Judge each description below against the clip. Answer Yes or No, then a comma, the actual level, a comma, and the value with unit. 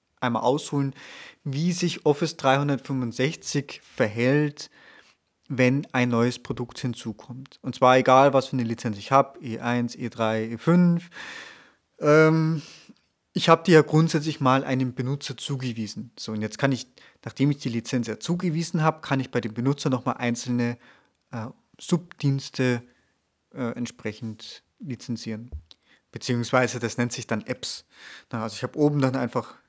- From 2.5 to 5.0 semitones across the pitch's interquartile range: Yes, average, 3.6 semitones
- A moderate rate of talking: Yes, average, 140 wpm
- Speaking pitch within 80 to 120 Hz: No, low, 130 Hz